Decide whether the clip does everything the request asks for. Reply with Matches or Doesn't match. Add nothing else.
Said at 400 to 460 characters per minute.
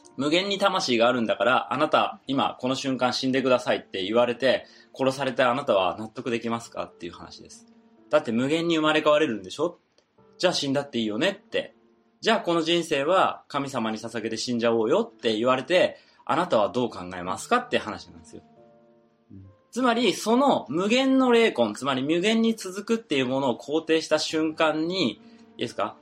Doesn't match